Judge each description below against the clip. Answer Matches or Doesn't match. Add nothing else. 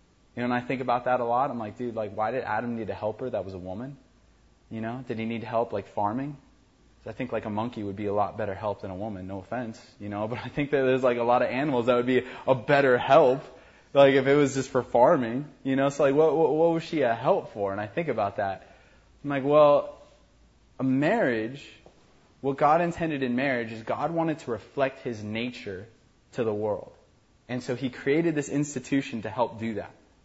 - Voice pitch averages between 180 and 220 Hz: Doesn't match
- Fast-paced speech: Matches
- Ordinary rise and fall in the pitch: Matches